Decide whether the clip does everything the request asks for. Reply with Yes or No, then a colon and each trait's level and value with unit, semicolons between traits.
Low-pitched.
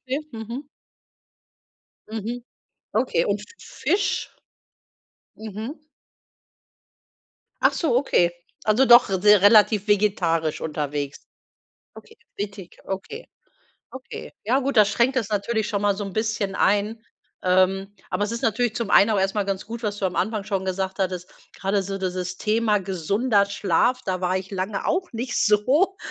No: high, 205 Hz